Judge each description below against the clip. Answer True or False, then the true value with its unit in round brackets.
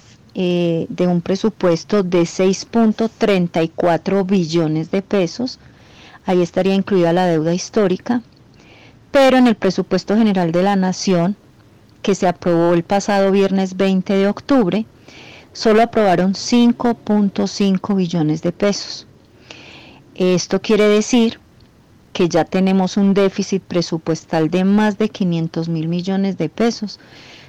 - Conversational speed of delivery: False (120 wpm)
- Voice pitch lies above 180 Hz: True (190 Hz)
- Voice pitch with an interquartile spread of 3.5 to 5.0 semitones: False (3.0 semitones)